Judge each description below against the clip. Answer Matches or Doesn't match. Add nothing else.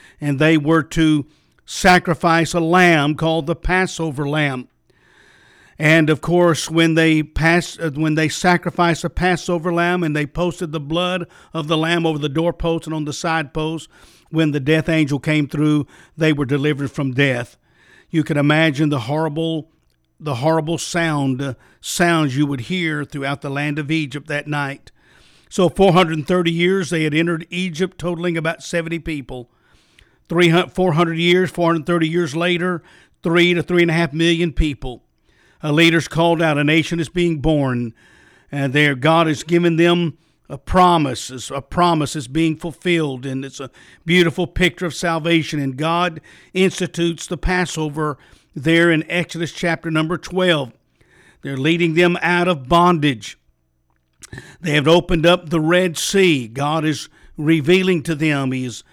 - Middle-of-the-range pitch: Matches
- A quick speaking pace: Doesn't match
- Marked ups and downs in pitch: Doesn't match